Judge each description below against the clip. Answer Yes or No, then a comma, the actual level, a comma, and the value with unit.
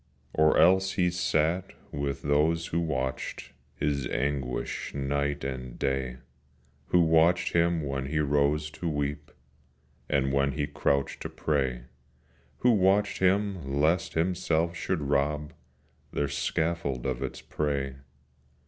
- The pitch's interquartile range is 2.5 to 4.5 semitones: Yes, average, 3.2 semitones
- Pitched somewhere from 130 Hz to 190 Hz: No, very low, 75 Hz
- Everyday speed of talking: No, slow, 125 wpm